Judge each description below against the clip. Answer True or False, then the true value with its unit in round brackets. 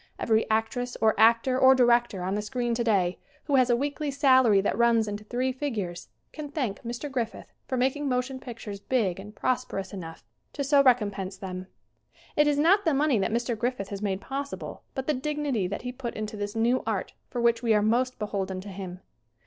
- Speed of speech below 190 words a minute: False (200 wpm)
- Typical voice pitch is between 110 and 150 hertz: False (235 Hz)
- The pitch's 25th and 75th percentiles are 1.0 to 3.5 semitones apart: False (4.2 semitones)